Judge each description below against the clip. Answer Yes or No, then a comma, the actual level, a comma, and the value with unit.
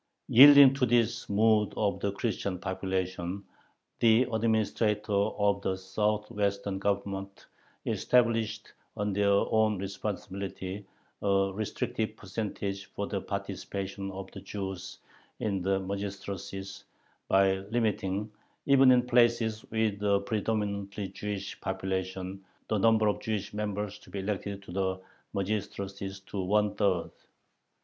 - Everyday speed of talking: No, slow, 115 wpm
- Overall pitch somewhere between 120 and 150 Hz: No, low, 100 Hz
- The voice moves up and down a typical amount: No, narrow, 1.9 semitones